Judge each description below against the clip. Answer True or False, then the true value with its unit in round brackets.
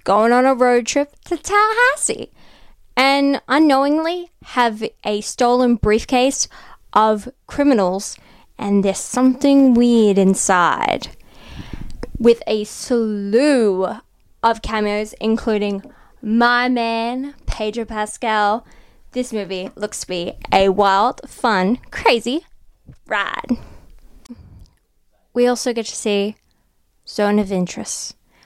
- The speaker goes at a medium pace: False (100 wpm)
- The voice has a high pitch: True (230 Hz)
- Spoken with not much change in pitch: False (3.6 semitones)